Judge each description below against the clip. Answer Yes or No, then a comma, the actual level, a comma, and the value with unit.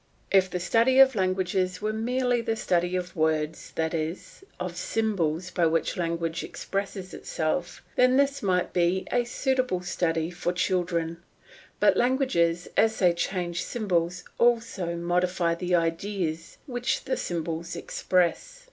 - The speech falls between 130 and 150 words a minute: Yes, average, 145 wpm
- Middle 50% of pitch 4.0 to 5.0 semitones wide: Yes, average, 4.4 semitones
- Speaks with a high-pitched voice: No, medium, 180 Hz